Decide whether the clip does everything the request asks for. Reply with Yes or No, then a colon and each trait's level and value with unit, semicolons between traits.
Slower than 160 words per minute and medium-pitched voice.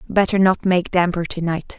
No: average, 200 wpm; medium, 180 Hz